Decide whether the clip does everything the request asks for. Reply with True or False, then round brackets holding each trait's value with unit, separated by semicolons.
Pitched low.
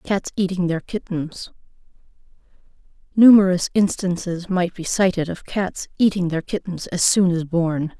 False (180 Hz)